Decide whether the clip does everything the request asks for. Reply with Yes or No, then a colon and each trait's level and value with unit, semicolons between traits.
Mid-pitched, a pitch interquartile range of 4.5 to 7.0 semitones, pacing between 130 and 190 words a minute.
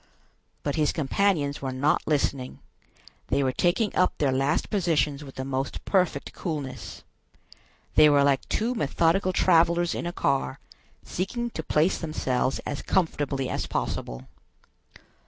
No: medium, 150 Hz; average, 4.1 semitones; average, 140 wpm